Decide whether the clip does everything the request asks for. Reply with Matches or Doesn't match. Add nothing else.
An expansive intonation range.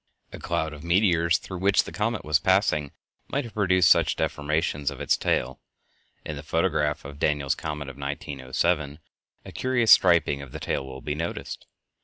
Doesn't match